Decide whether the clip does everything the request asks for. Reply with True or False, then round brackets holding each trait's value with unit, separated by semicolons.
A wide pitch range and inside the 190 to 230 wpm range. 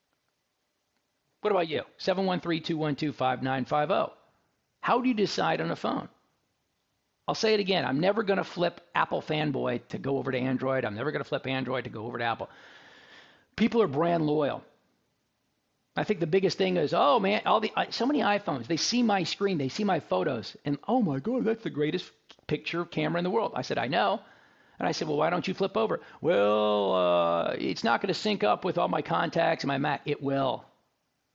True (6.7 semitones; 205 wpm)